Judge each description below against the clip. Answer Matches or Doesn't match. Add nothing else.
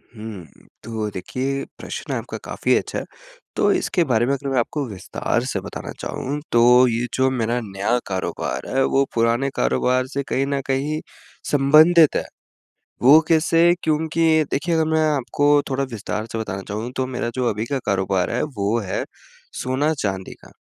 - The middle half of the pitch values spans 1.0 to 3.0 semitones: Doesn't match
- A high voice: Doesn't match